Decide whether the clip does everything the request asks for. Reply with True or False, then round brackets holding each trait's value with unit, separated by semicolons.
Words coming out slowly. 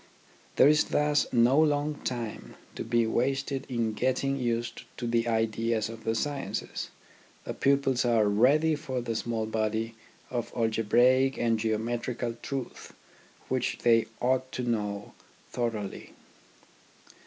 True (130 wpm)